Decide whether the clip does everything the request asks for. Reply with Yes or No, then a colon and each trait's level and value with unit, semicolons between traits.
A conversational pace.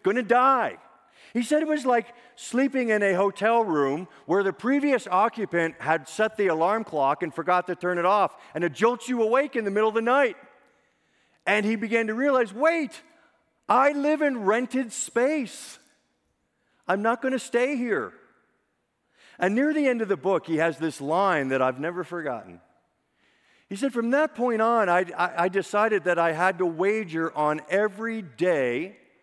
Yes: average, 185 wpm